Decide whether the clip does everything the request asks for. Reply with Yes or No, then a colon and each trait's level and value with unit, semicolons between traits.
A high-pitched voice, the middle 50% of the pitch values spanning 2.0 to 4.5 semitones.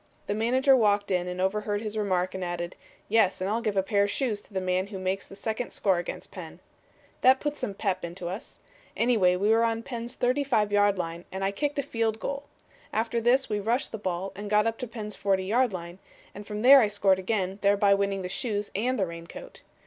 Yes: high, 205 Hz; average, 3.3 semitones